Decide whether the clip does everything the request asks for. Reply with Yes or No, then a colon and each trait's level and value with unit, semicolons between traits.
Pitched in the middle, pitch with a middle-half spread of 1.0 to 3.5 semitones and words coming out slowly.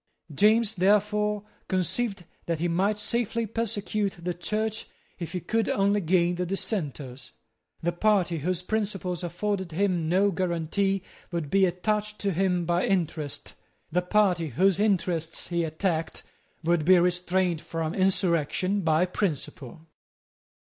Yes: medium, 180 Hz; average, 3.1 semitones; slow, 130 wpm